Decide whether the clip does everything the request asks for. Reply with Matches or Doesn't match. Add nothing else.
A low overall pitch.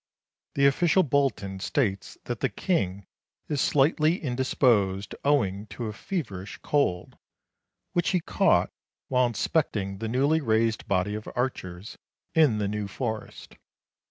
Matches